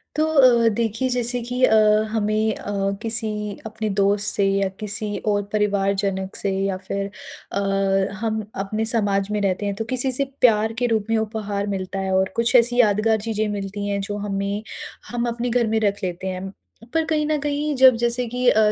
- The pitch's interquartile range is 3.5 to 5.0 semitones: No, average, 2.8 semitones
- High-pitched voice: Yes, high, 215 Hz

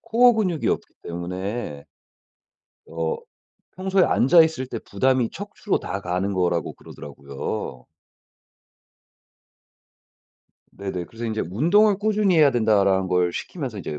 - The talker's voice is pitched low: Yes, low, 110 Hz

